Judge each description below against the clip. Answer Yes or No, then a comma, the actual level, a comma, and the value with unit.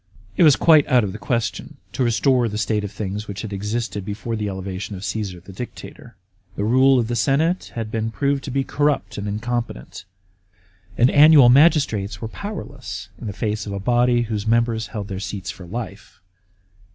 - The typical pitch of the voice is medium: No, low, 110 Hz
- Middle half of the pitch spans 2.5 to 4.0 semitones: Yes, average, 3.7 semitones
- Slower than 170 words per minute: No, average, 190 wpm